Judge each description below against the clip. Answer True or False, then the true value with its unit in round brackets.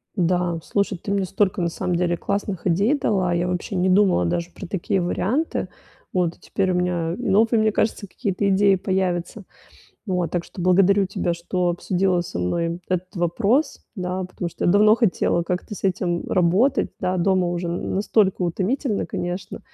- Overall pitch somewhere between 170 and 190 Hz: True (185 Hz)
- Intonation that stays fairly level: True (2.3 semitones)